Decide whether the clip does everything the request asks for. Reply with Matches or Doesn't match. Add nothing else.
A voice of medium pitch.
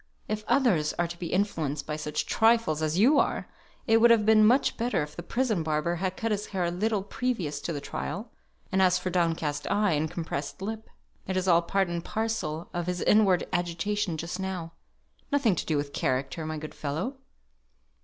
Matches